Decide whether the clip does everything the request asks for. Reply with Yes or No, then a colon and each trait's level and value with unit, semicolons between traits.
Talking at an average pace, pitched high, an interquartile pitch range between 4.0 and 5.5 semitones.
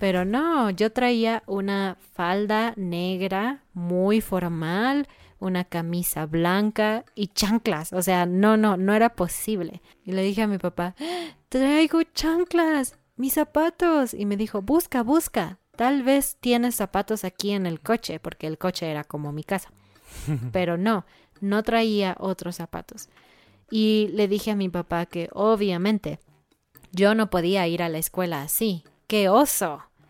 Yes: average, 150 wpm; high, 200 Hz; average, 4.3 semitones